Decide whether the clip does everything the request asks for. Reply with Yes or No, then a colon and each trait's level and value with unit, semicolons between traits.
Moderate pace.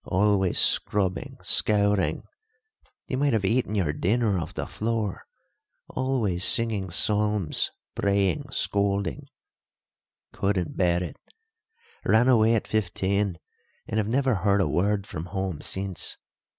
No: slow, 120 wpm